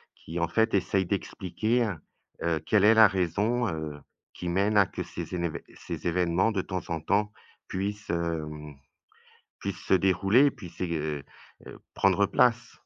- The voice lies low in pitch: Yes, very low, 95 Hz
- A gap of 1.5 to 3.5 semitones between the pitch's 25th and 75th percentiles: No, average, 3.9 semitones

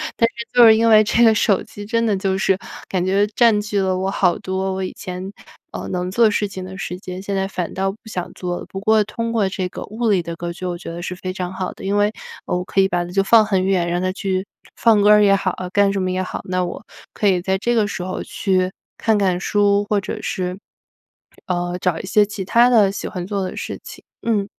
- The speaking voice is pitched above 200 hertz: No, high, 195 Hz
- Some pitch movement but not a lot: No, narrow, 2.1 semitones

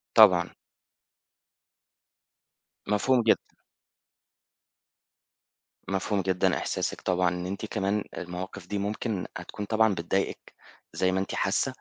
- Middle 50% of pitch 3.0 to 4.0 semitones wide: No, narrow, 2.4 semitones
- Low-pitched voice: Yes, very low, 95 Hz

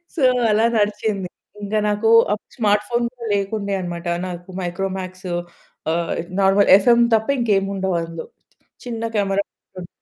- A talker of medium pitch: No, high, 200 Hz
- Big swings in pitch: No, average, 2.7 semitones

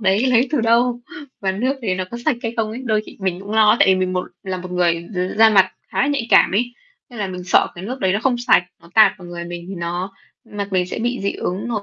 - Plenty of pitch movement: No, average, 4.2 semitones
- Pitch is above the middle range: Yes, high, 200 Hz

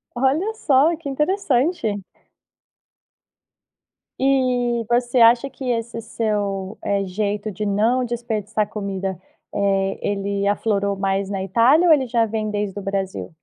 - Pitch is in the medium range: No, high, 220 Hz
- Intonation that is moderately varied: Yes, average, 4.0 semitones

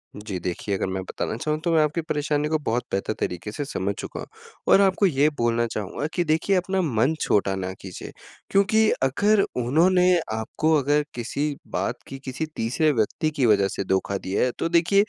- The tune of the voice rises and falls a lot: Yes, wide, 7.4 semitones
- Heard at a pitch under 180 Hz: Yes, medium, 140 Hz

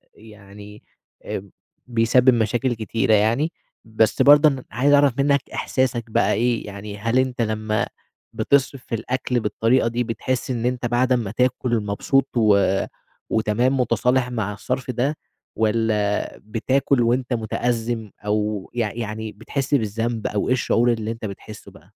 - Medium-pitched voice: No, low, 115 Hz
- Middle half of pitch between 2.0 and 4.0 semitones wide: Yes, average, 2.8 semitones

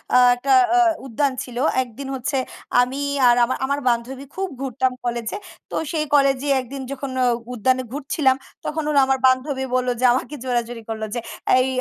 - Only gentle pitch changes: Yes, narrow, 2.0 semitones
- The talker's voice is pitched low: No, very high, 260 Hz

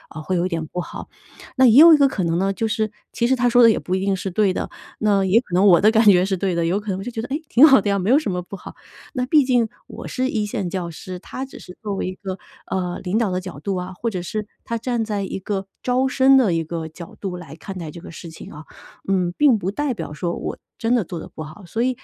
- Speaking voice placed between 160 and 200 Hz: Yes, high, 195 Hz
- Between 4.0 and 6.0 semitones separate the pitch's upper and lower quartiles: Yes, average, 4.7 semitones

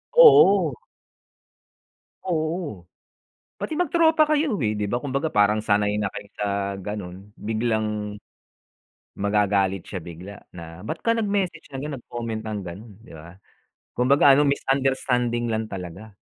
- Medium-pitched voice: No, low, 110 Hz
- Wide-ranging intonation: Yes, wide, 6.5 semitones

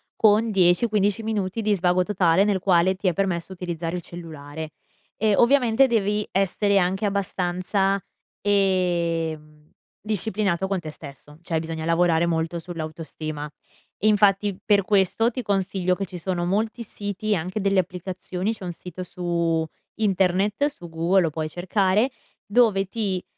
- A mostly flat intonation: No, average, 3.1 semitones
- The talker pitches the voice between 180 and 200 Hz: Yes, medium, 185 Hz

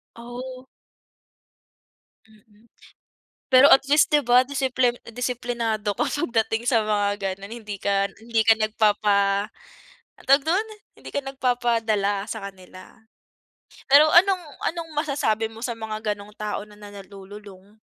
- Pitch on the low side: No, high, 225 Hz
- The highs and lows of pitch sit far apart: No, average, 3.6 semitones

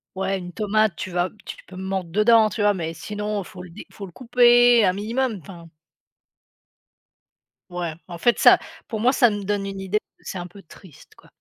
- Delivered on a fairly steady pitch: No, average, 3.1 semitones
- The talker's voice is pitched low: No, high, 195 Hz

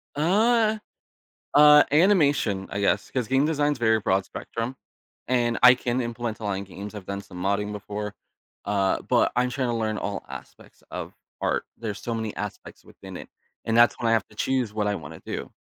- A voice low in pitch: Yes, low, 115 Hz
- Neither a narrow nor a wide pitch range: Yes, average, 4.4 semitones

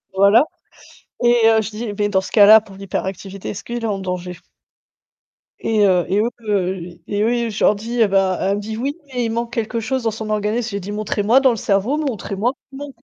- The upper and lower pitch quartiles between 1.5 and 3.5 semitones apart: Yes, average, 2.9 semitones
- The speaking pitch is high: Yes, high, 215 Hz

